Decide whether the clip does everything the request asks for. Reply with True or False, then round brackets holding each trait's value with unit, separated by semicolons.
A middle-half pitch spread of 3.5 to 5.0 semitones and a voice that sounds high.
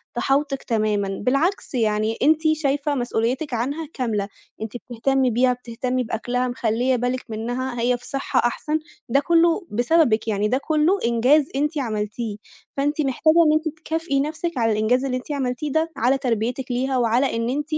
True (3.9 semitones; 255 Hz)